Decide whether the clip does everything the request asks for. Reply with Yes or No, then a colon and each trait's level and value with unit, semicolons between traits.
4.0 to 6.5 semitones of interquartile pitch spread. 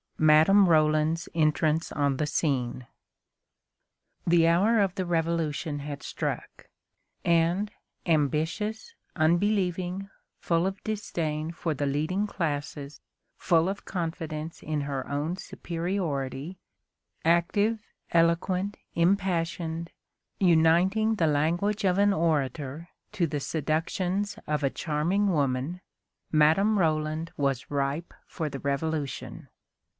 No: average, 3.5 semitones